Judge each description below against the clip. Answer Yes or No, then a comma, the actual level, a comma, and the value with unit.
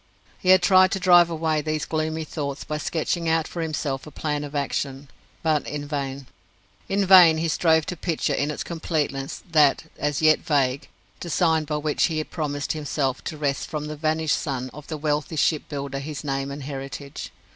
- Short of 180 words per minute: No, average, 190 wpm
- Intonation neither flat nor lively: No, narrow, 2.2 semitones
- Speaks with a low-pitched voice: No, medium, 150 Hz